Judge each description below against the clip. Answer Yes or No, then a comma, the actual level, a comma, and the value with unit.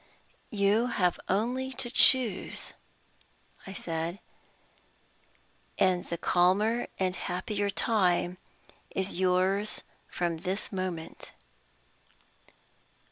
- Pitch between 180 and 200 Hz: Yes, high, 190 Hz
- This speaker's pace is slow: Yes, slow, 80 wpm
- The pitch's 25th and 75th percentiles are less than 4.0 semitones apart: Yes, average, 2.9 semitones